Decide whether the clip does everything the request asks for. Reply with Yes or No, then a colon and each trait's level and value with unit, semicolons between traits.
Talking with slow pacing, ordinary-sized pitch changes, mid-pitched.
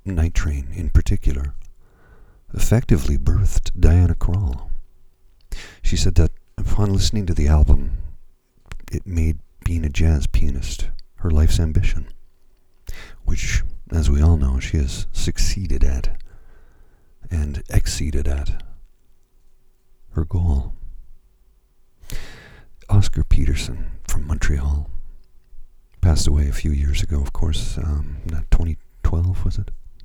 No: slow, 110 wpm; average, 3.5 semitones; very low, 80 Hz